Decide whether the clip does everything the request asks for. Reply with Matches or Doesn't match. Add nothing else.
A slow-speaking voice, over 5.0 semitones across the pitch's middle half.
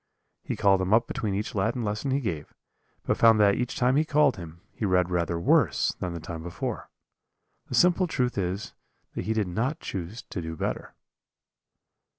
Doesn't match